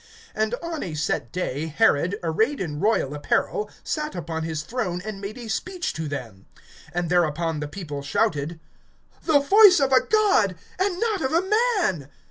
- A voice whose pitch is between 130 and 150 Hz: No, high, 190 Hz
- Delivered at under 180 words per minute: Yes, average, 170 wpm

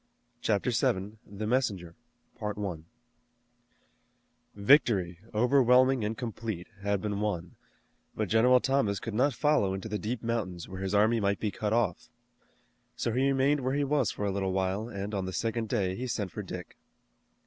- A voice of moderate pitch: No, low, 105 Hz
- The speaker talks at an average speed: Yes, average, 160 wpm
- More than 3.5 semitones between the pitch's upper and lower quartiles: Yes, average, 4.0 semitones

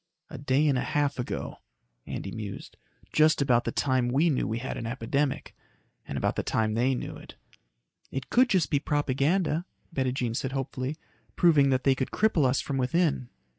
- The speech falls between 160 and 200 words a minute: Yes, average, 175 wpm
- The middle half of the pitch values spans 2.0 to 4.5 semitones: Yes, average, 2.9 semitones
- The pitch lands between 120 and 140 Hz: Yes, low, 135 Hz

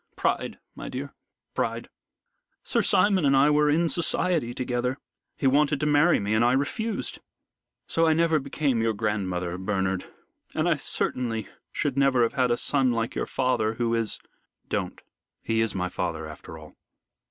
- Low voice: Yes, low, 125 Hz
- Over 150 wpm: Yes, average, 170 wpm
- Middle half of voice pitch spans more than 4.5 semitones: Yes, average, 4.9 semitones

